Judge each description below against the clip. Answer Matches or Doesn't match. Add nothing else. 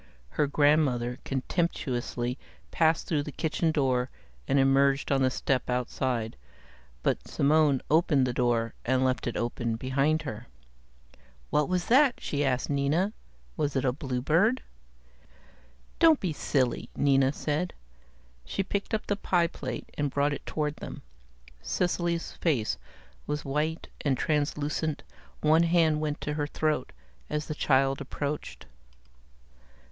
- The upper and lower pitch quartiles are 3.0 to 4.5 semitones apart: Matches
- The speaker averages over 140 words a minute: Doesn't match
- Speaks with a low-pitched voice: Doesn't match